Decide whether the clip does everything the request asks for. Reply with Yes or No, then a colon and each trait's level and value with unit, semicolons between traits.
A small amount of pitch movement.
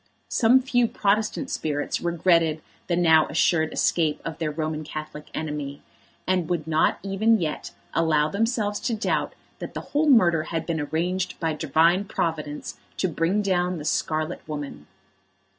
No: average, 4.0 semitones